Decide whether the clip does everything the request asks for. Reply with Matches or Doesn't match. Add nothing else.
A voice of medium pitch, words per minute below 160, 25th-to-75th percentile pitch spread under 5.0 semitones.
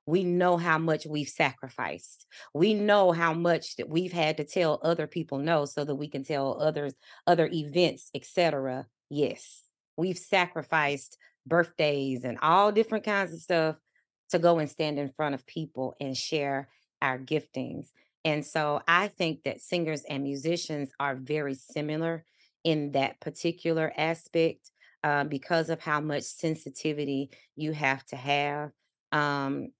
Matches